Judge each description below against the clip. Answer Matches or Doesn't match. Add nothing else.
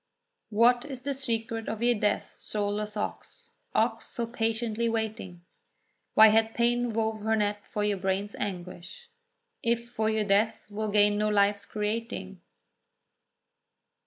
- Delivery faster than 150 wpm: Doesn't match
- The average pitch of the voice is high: Matches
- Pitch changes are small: Matches